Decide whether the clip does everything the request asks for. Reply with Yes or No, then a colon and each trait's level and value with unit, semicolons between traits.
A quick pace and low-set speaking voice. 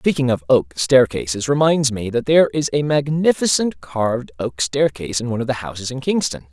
No: average, 195 wpm; low, 130 Hz